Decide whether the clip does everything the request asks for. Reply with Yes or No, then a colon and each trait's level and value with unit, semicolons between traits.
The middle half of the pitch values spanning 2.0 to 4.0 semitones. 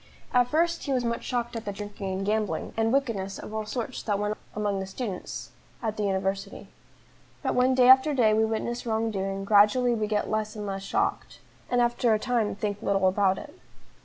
Yes: average, 3.1 semitones